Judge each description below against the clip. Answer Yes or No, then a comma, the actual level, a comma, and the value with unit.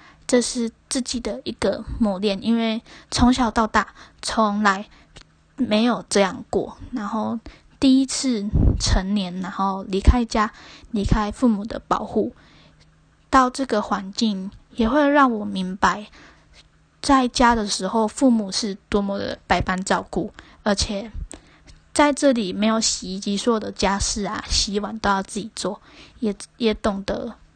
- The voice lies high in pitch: Yes, high, 220 Hz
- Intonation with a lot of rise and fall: No, average, 3.3 semitones